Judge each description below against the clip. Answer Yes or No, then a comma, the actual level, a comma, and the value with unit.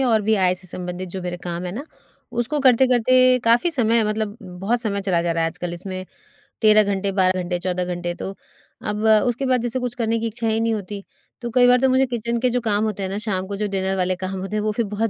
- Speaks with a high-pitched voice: Yes, high, 210 Hz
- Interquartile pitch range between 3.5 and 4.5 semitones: Yes, average, 4.1 semitones